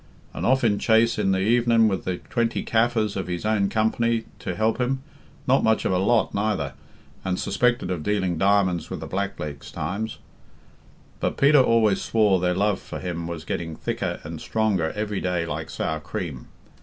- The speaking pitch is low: Yes, low, 100 Hz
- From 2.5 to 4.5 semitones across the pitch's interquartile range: Yes, average, 4.0 semitones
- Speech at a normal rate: Yes, average, 180 wpm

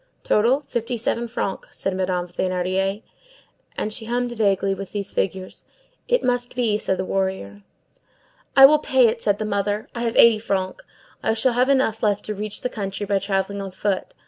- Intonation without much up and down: No, average, 3.5 semitones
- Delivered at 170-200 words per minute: Yes, average, 185 wpm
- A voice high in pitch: Yes, high, 210 Hz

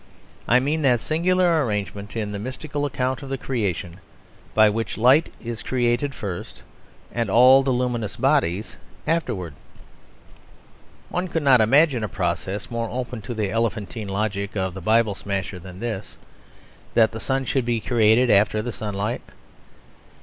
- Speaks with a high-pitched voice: No, low, 115 Hz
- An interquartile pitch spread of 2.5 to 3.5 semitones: No, average, 4.2 semitones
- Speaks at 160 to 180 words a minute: No, average, 150 wpm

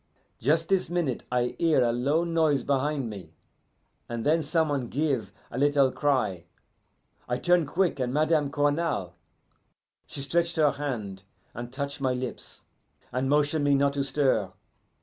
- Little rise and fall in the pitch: No, average, 3.7 semitones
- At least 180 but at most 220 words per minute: No, average, 150 wpm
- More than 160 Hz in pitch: No, medium, 140 Hz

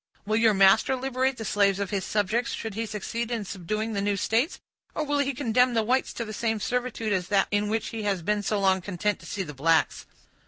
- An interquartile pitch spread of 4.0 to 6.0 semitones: No, average, 2.9 semitones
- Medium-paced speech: No, fast, 235 wpm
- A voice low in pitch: No, high, 215 Hz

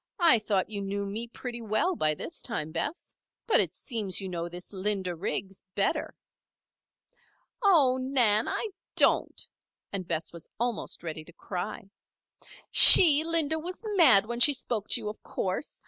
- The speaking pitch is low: No, high, 215 Hz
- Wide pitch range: Yes, wide, 6.1 semitones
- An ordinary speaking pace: Yes, average, 160 wpm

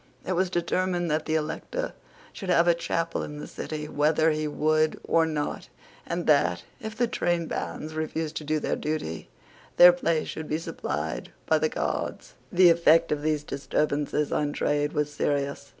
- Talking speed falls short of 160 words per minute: No, average, 170 wpm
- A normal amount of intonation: No, narrow, 2.2 semitones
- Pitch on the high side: No, medium, 155 Hz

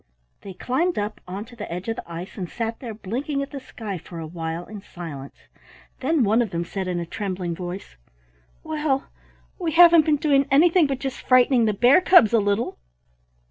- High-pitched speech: Yes, high, 225 Hz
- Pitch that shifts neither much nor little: No, wide, 7.2 semitones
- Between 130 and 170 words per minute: No, average, 195 wpm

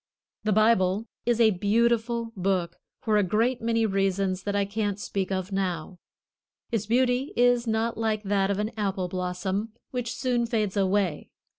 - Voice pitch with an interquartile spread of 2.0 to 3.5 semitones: Yes, average, 3.1 semitones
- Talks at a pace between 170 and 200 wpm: No, average, 160 wpm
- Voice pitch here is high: Yes, high, 210 Hz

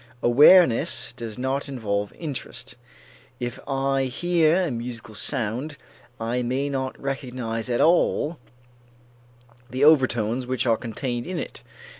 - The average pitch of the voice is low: Yes, low, 130 Hz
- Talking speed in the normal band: No, slow, 120 wpm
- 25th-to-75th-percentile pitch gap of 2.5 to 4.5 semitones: Yes, average, 3.0 semitones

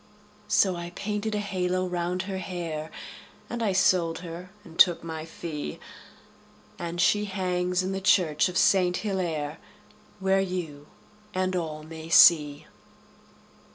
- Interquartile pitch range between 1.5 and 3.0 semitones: Yes, narrow, 2.4 semitones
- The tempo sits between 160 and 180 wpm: No, slow, 135 wpm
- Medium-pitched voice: Yes, medium, 180 Hz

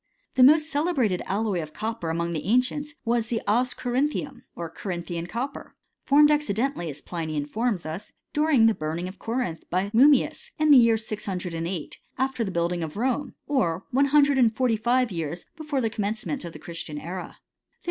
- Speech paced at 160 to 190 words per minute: Yes, average, 180 wpm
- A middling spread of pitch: No, wide, 7.4 semitones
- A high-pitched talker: Yes, high, 225 Hz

